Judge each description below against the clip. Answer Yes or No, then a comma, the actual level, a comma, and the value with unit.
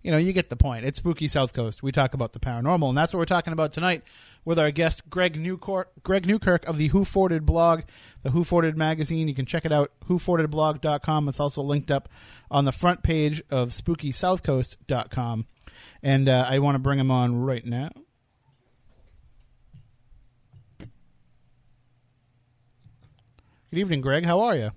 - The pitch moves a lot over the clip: No, average, 5.0 semitones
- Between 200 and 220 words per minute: No, average, 170 wpm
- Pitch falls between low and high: Yes, medium, 145 Hz